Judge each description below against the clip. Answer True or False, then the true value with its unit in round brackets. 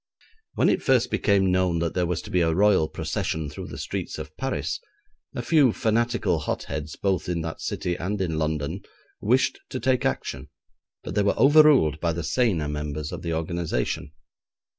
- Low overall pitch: True (90 Hz)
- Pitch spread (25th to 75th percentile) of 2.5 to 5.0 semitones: False (5.6 semitones)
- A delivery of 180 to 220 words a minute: True (185 wpm)